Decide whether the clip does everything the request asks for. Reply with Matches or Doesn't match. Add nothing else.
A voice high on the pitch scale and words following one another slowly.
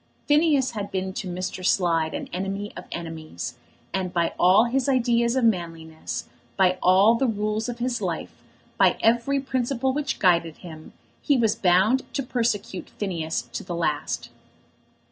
Doesn't match